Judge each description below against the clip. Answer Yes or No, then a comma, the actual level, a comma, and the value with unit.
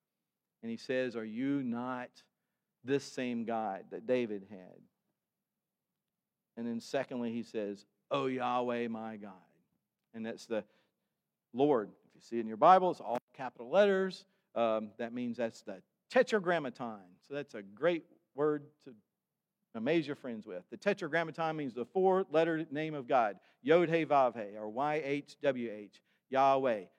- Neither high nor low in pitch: No, low, 130 Hz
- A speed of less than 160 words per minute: Yes, average, 150 wpm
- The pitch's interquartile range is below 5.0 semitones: No, wide, 5.6 semitones